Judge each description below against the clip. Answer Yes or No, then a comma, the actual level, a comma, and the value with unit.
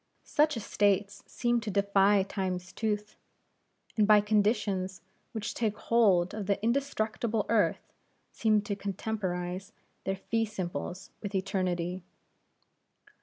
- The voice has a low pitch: No, high, 205 Hz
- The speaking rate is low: Yes, slow, 115 wpm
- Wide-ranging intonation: No, narrow, 2.4 semitones